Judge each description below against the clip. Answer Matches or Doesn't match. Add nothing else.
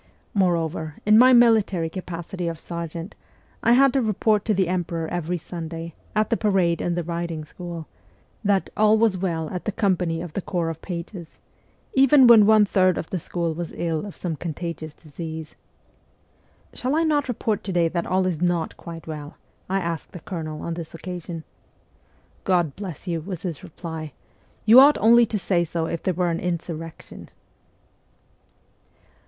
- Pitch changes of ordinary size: Matches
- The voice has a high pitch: Doesn't match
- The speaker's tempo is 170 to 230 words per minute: Matches